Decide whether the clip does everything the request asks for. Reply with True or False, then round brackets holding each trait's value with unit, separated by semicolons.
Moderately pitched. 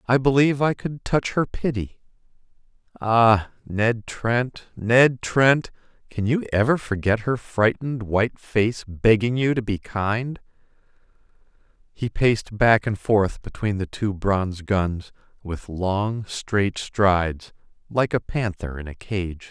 False (110 Hz)